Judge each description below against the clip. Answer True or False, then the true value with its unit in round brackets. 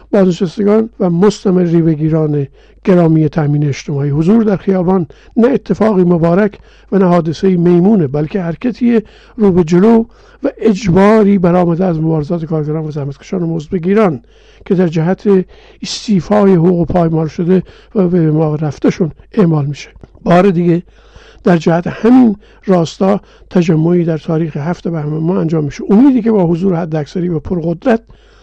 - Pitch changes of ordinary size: True (3.6 semitones)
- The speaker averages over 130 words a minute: True (140 wpm)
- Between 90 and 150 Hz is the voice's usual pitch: False (180 Hz)